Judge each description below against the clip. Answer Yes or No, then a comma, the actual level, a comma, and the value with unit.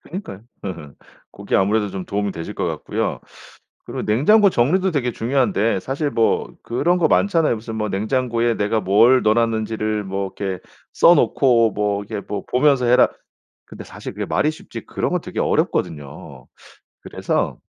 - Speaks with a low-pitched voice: Yes, low, 115 Hz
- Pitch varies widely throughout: No, average, 4.5 semitones